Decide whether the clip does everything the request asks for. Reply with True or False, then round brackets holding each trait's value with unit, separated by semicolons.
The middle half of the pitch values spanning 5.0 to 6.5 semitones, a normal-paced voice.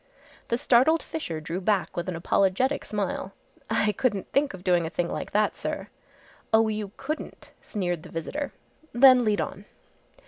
True (5.4 semitones; 165 wpm)